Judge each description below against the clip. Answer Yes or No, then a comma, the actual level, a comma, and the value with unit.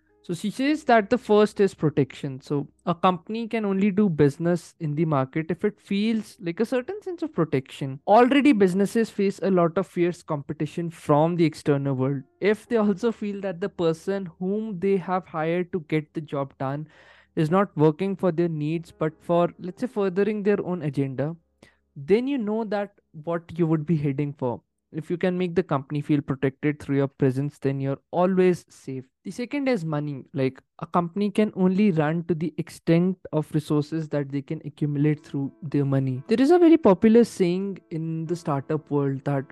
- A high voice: No, medium, 170 Hz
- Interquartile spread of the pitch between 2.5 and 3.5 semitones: No, average, 5.2 semitones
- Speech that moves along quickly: Yes, fast, 195 wpm